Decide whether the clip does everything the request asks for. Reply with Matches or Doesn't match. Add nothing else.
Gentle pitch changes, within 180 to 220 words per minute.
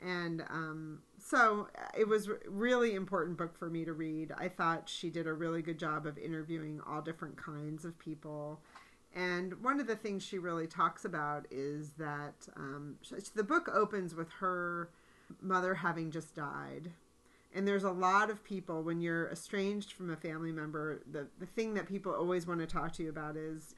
Doesn't match